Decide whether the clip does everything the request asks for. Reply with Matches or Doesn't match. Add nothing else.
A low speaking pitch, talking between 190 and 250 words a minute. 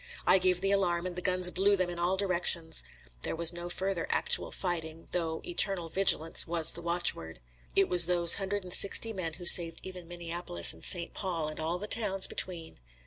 Doesn't match